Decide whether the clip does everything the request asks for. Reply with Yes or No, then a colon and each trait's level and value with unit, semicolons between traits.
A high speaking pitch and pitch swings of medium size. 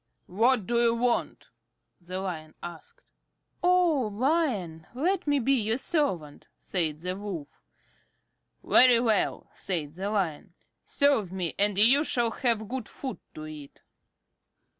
No: high, 215 Hz; wide, 6.6 semitones